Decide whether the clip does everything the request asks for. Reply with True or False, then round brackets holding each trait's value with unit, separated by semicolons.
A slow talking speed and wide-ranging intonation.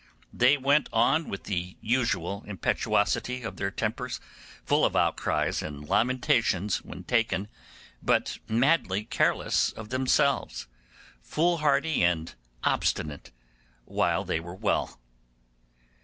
True (110 wpm; 6.1 semitones)